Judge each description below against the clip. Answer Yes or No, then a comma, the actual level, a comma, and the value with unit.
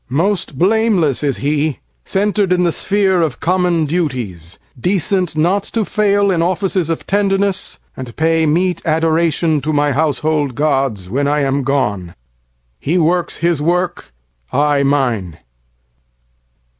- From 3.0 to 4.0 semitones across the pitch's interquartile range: No, average, 4.4 semitones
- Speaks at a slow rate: Yes, slow, 120 wpm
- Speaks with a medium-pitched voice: Yes, medium, 160 Hz